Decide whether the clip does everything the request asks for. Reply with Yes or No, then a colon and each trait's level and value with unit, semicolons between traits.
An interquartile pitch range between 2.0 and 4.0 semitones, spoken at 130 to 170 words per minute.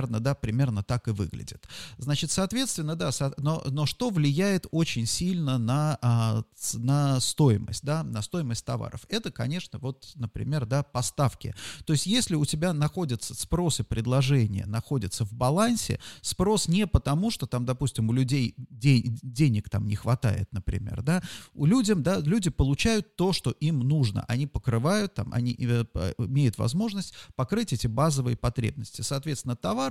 No: average, 5.1 semitones; average, 155 wpm